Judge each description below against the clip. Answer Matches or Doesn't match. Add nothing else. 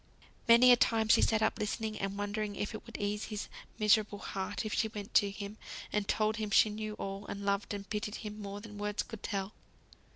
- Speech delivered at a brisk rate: Matches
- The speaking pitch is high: Matches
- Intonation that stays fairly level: Matches